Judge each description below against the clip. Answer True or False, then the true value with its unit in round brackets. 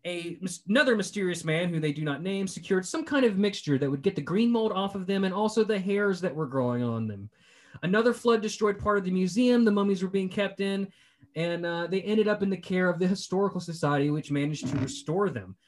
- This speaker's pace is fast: True (235 wpm)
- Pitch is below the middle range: False (190 Hz)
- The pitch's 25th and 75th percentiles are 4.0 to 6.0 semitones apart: True (4.3 semitones)